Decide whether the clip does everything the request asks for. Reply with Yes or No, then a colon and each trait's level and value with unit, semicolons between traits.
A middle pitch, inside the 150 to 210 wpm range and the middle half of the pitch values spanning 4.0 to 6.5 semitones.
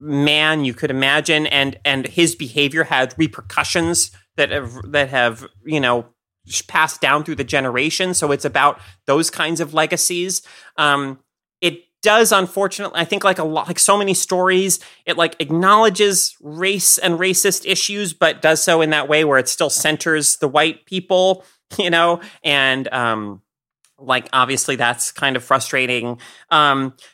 Yes: medium, 150 Hz; average, 160 wpm; average, 4.6 semitones